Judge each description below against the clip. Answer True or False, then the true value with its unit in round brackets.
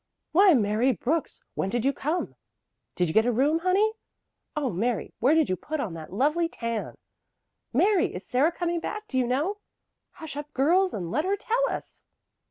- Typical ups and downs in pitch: False (6.8 semitones)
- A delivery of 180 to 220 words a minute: True (185 wpm)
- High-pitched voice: True (290 Hz)